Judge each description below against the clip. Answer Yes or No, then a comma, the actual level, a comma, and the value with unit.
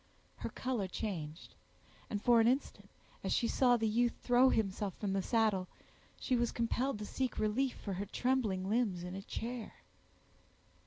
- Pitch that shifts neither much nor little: Yes, average, 3.8 semitones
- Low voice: No, high, 225 Hz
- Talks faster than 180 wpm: No, average, 165 wpm